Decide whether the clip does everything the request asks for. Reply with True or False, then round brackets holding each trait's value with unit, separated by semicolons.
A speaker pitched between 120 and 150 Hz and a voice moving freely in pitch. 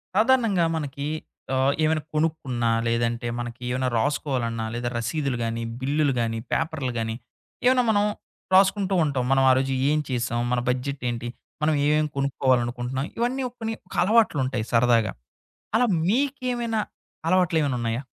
True (135 Hz; 6.4 semitones)